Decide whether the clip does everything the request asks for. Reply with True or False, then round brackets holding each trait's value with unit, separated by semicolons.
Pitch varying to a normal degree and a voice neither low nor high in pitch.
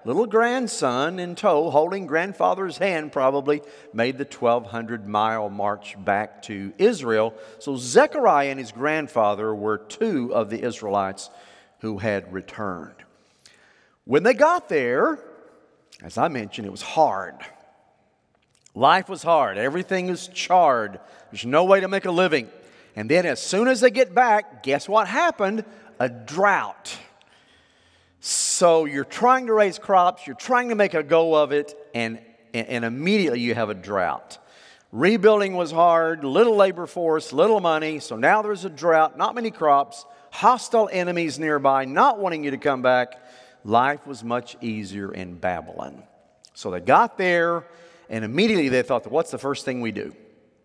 False (8.5 semitones; 150 Hz)